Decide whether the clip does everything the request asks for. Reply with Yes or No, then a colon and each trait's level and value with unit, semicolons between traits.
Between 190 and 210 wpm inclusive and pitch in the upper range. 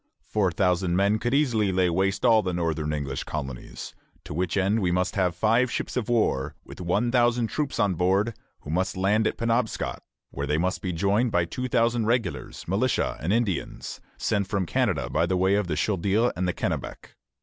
No: average, 195 wpm; very low, 95 Hz